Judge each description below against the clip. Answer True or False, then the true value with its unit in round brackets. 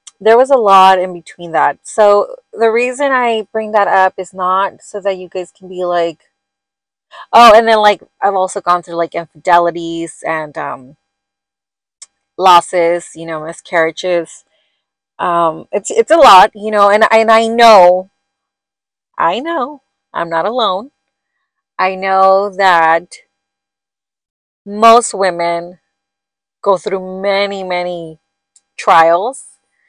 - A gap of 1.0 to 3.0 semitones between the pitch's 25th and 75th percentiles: False (3.8 semitones)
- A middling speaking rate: False (130 wpm)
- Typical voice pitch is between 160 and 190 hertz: True (185 Hz)